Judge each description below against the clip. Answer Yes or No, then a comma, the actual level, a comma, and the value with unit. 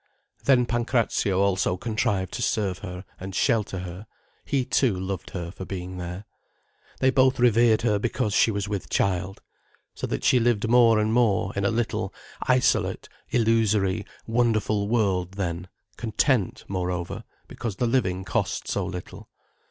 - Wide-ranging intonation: No, average, 3.9 semitones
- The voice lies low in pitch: Yes, low, 105 Hz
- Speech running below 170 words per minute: Yes, average, 150 wpm